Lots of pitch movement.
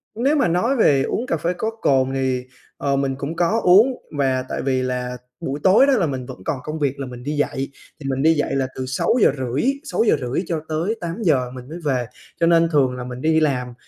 No: average, 4.6 semitones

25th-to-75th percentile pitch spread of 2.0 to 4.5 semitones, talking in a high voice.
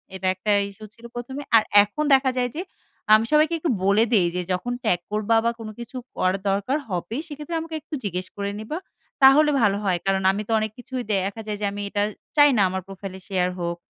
No: average, 5.1 semitones; high, 215 Hz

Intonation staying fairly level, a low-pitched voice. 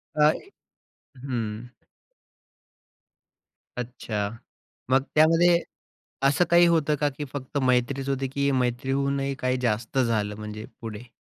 No: average, 3.5 semitones; low, 130 Hz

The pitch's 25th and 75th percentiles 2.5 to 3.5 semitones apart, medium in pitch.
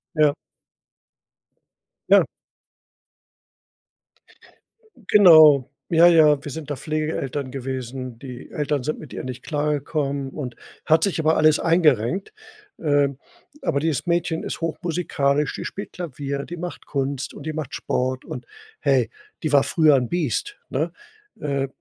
Yes: average, 2.9 semitones; medium, 150 Hz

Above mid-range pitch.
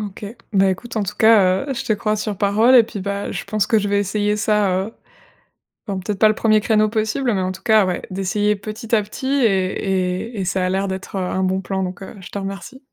Yes: high, 205 Hz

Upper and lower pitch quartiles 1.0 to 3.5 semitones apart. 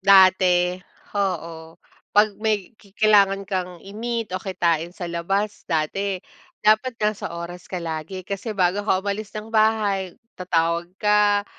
Yes: average, 2.8 semitones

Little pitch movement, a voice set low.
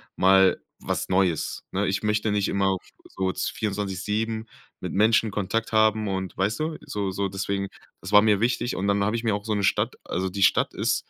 Yes: narrow, 2.2 semitones; low, 100 Hz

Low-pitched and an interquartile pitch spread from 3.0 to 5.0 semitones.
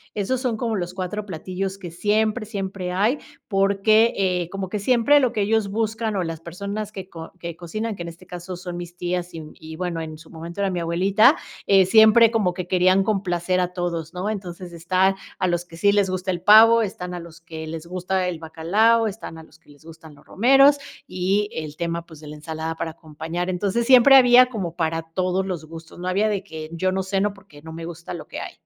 No: medium, 185 Hz; average, 3.6 semitones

